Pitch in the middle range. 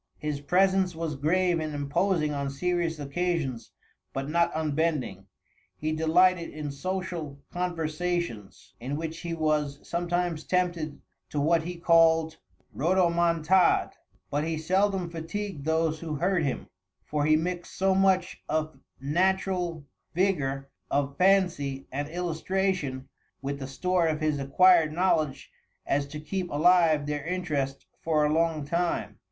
Yes: medium, 160 Hz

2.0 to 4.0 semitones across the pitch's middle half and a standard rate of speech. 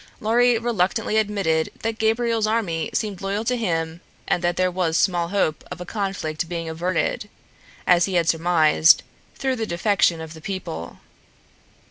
No: average, 4.6 semitones; average, 155 wpm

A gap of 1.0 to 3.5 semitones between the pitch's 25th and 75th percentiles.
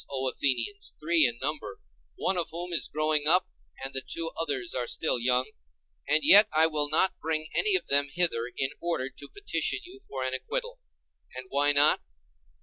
No: average, 4.5 semitones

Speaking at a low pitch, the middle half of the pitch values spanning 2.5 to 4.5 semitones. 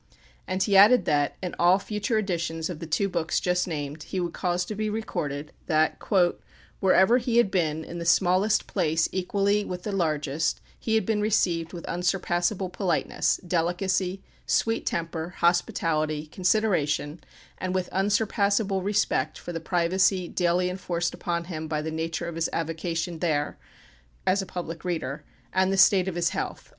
No: medium, 180 Hz; average, 2.9 semitones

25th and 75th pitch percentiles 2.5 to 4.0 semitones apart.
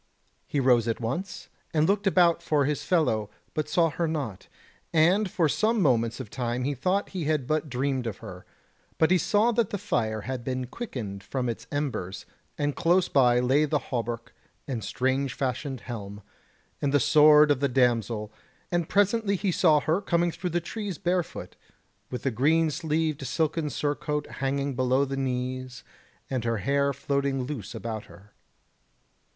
No: average, 4.9 semitones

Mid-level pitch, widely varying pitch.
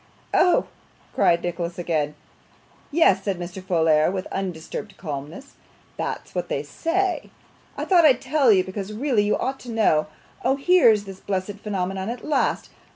No: high, 195 Hz; wide, 6.7 semitones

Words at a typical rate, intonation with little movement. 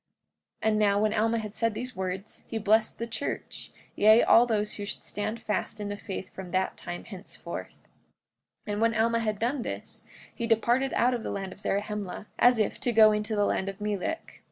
No: fast, 210 wpm; narrow, 1.9 semitones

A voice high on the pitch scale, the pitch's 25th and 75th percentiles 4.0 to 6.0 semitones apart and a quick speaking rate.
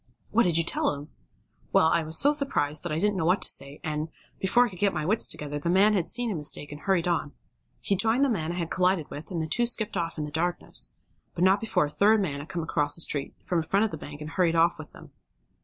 No: medium, 170 Hz; average, 4.6 semitones; fast, 280 wpm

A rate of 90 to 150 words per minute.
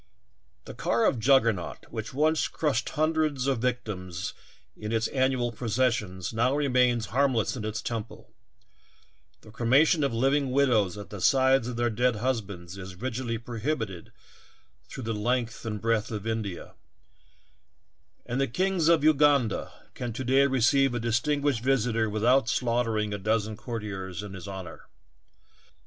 Yes: average, 145 wpm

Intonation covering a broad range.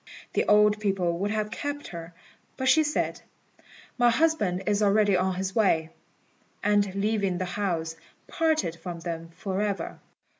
No: average, 3.1 semitones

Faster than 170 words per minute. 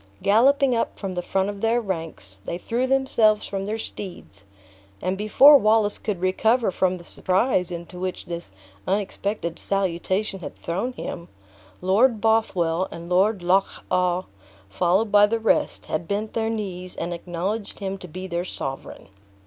No: average, 155 wpm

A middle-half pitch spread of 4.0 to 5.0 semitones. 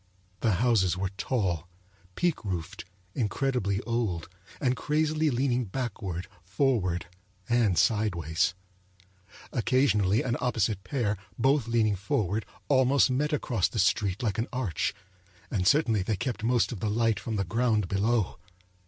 Yes: average, 4.7 semitones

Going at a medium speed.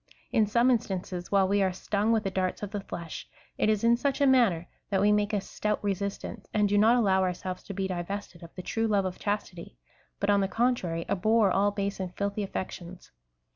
No: fast, 215 wpm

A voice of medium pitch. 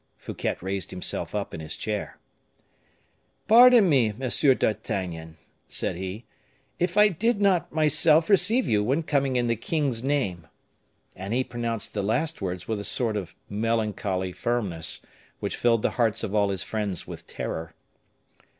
No: low, 115 Hz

